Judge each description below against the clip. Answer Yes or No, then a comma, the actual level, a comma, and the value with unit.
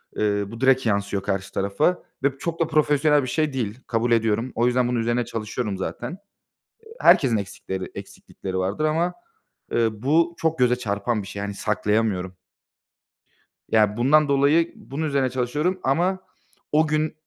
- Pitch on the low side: Yes, low, 125 Hz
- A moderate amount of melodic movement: No, wide, 6.3 semitones